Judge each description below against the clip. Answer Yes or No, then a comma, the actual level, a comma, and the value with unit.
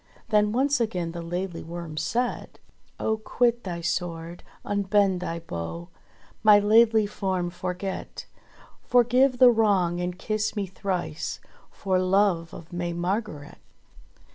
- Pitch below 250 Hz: Yes, high, 190 Hz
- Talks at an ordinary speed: No, slow, 125 wpm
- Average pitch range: Yes, average, 3.8 semitones